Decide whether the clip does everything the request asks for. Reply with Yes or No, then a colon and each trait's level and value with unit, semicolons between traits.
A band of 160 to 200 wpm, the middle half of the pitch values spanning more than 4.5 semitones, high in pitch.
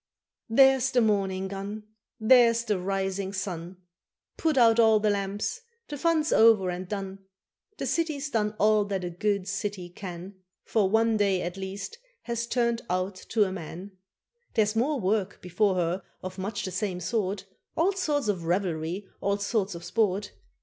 No: average, 165 wpm; average, 3.2 semitones; high, 205 Hz